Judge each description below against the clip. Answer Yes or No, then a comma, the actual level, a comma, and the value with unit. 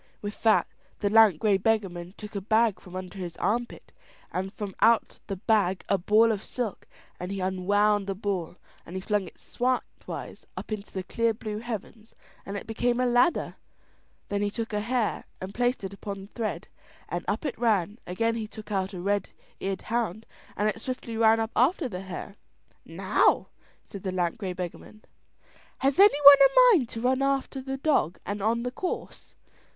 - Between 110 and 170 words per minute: No, average, 190 wpm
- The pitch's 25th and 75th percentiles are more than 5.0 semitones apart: No, average, 3.4 semitones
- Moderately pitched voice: No, high, 215 Hz